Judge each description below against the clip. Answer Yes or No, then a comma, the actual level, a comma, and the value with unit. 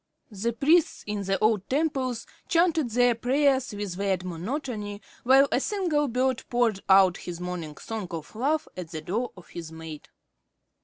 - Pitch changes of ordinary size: No, wide, 6.5 semitones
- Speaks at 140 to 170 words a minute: Yes, average, 160 wpm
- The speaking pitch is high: Yes, high, 225 Hz